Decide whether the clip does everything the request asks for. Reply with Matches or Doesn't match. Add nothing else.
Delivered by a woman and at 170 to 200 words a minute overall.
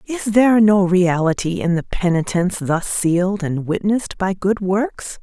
Doesn't match